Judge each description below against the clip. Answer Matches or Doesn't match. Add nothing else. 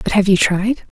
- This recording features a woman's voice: Matches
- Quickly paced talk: Matches